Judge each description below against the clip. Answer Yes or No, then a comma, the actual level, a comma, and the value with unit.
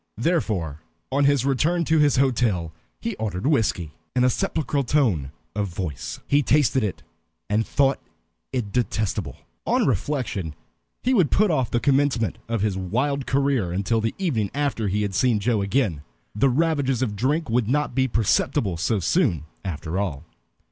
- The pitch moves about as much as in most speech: No, wide, 6.1 semitones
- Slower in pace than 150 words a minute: No, average, 160 wpm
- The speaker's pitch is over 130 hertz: No, low, 120 Hz